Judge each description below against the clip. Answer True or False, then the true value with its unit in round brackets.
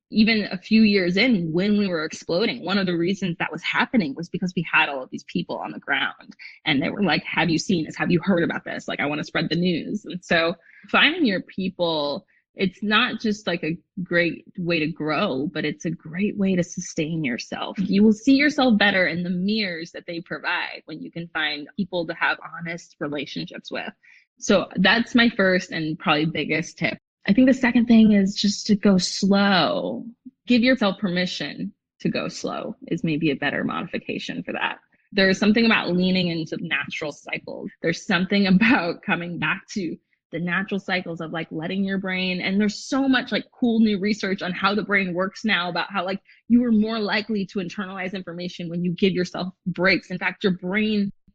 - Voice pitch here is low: False (190 Hz)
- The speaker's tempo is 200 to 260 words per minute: True (205 wpm)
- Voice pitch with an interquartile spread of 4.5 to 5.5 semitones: False (3.7 semitones)